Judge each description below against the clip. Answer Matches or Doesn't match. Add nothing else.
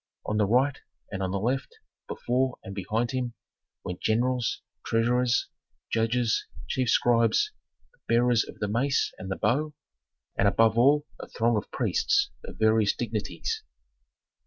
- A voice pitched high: Doesn't match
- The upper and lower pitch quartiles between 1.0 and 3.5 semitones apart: Matches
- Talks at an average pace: Matches